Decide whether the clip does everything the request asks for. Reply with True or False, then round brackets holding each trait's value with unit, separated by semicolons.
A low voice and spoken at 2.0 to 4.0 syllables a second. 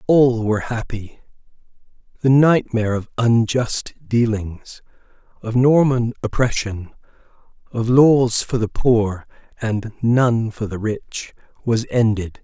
True (115 Hz; 3.7 syllables/s)